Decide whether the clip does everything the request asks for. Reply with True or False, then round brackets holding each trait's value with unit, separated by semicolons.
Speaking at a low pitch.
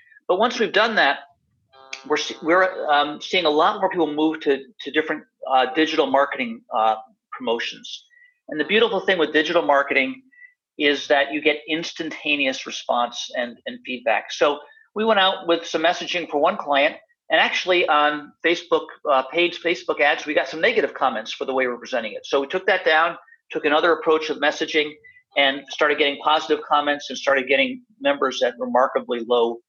False (155 Hz)